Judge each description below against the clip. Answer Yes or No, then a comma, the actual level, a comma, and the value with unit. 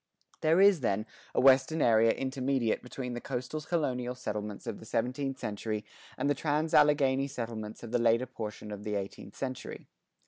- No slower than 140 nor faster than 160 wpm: No, average, 170 wpm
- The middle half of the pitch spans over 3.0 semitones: Yes, average, 3.7 semitones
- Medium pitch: No, low, 125 Hz